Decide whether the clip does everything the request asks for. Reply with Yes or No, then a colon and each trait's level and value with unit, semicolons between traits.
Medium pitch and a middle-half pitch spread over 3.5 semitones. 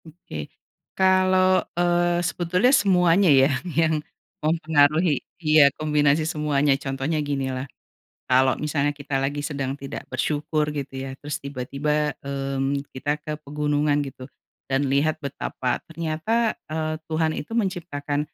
No: medium, 150 Hz; average, 2.8 semitones